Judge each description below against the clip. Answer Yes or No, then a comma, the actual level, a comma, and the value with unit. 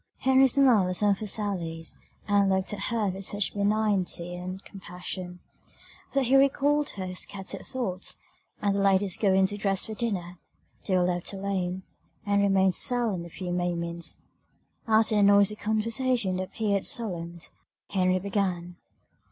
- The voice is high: Yes, high, 195 Hz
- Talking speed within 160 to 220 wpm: No, average, 150 wpm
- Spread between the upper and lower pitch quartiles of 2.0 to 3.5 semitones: Yes, average, 2.8 semitones